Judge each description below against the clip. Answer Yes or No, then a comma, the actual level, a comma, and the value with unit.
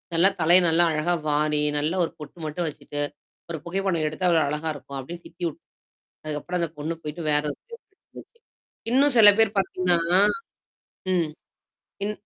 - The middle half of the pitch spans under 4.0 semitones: Yes, average, 3.3 semitones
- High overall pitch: No, medium, 170 Hz